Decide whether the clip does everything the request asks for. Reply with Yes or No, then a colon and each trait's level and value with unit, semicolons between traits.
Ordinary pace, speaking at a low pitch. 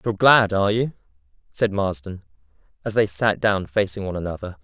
Yes: average, 170 wpm; low, 100 Hz